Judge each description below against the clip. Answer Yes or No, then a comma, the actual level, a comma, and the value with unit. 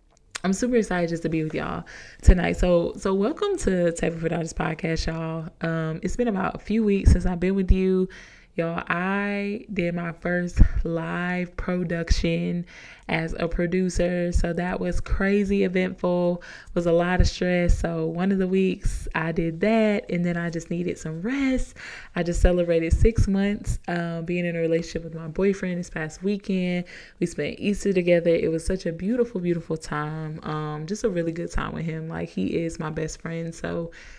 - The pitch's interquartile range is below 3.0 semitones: Yes, narrow, 2.4 semitones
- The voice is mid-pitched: Yes, medium, 175 Hz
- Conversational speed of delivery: Yes, average, 190 wpm